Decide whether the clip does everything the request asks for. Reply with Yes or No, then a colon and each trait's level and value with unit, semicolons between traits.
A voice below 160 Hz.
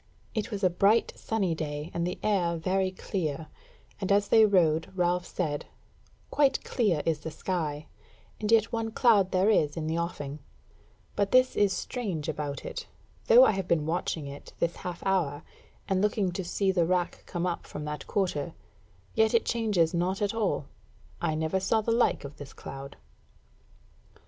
No: medium, 180 Hz